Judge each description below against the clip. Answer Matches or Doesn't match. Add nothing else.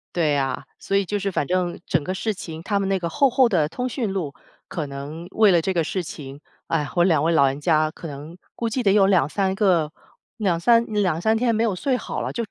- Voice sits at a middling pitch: Matches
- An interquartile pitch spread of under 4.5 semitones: Doesn't match